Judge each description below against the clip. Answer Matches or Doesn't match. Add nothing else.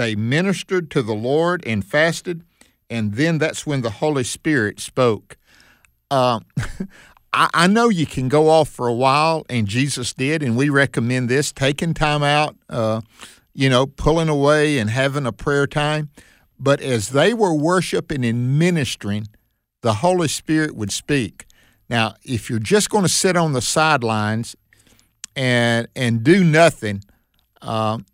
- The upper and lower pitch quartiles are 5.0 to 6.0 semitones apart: Matches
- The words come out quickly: Doesn't match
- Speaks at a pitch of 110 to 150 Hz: Matches